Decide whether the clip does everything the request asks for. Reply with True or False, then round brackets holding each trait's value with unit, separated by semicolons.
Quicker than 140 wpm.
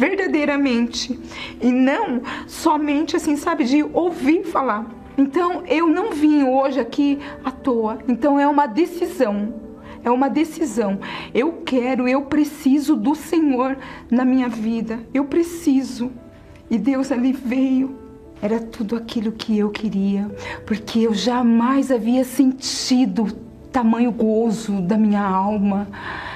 False (125 wpm)